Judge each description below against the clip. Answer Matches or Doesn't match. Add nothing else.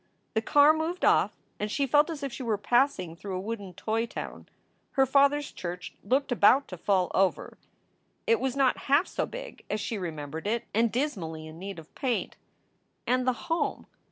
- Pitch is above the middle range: Matches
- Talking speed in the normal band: Matches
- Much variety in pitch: Matches